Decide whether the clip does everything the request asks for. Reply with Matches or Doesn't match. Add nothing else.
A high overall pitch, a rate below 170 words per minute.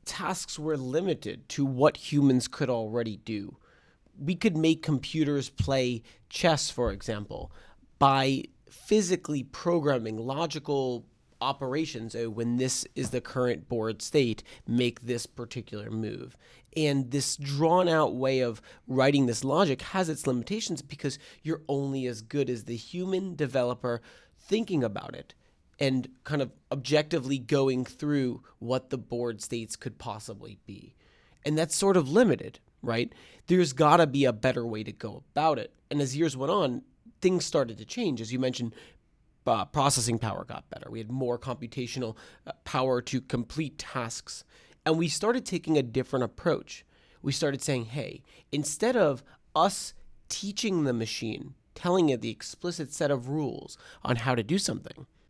Doesn't match